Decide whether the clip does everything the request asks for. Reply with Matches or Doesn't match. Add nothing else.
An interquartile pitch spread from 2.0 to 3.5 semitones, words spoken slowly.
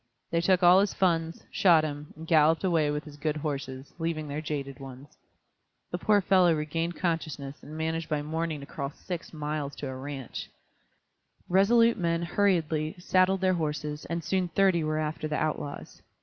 Doesn't match